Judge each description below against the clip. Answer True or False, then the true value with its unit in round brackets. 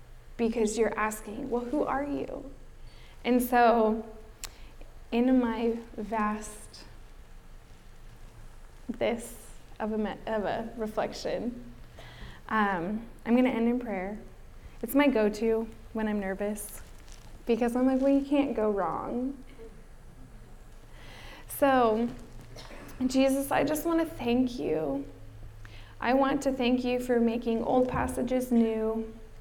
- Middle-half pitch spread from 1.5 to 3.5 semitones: True (2.9 semitones)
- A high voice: True (230 Hz)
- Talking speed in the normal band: False (120 wpm)